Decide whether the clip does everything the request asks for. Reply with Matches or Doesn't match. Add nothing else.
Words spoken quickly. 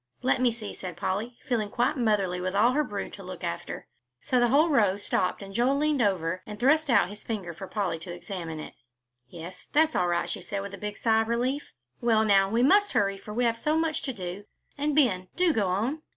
Matches